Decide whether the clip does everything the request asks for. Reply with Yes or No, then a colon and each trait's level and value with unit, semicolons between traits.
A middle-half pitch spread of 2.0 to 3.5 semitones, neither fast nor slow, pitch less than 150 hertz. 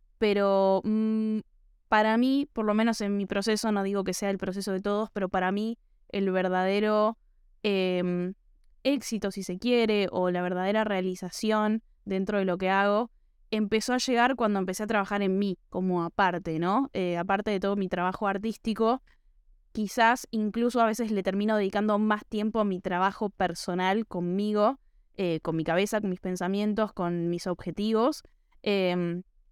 No: average, 2.7 semitones; average, 165 wpm; high, 200 Hz